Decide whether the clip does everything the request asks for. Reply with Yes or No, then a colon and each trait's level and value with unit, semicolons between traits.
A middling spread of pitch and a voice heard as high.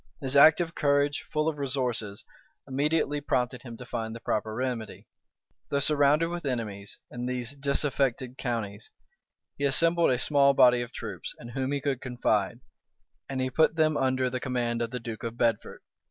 No: average, 3.2 semitones; low, 130 Hz